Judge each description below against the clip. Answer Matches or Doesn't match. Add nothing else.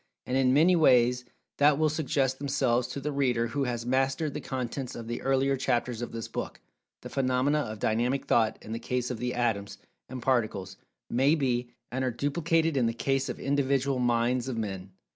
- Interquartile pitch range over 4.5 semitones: Doesn't match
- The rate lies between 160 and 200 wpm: Matches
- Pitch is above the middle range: Doesn't match